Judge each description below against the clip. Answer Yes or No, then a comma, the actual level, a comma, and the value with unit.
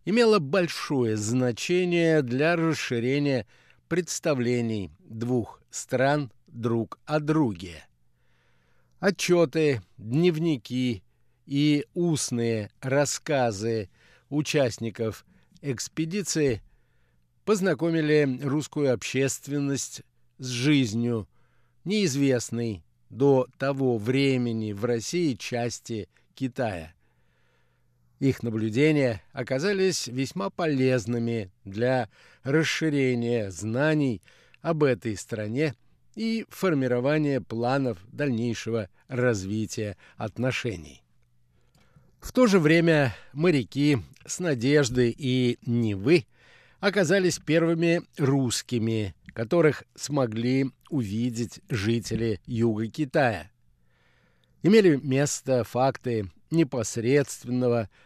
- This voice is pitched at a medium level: No, low, 125 Hz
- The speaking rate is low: Yes, slow, 70 wpm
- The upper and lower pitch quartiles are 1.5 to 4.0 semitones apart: No, average, 4.6 semitones